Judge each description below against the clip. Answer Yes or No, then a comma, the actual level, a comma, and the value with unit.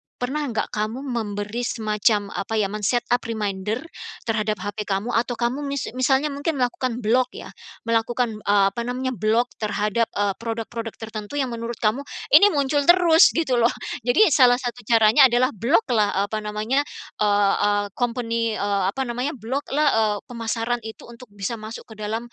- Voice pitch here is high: Yes, high, 230 Hz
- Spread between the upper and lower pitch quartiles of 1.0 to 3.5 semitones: Yes, average, 3.0 semitones